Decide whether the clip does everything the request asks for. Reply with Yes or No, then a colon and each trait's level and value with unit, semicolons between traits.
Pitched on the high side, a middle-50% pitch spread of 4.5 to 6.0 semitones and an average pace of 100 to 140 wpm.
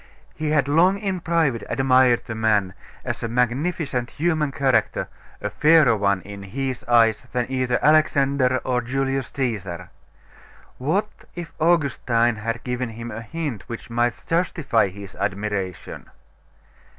No: low, 125 Hz; average, 4.8 semitones; slow, 135 wpm